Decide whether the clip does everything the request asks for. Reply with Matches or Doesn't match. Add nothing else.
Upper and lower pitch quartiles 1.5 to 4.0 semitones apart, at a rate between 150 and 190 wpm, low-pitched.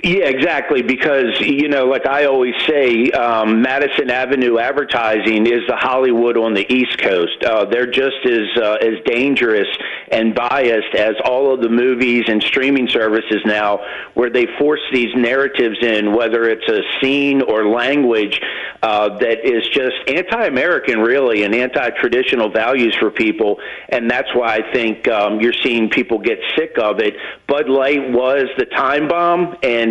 Matches